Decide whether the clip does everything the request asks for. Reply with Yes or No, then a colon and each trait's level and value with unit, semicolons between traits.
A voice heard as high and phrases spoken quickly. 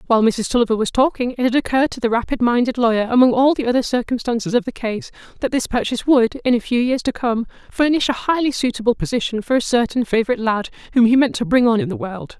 Yes: high, 240 Hz; fast, 240 wpm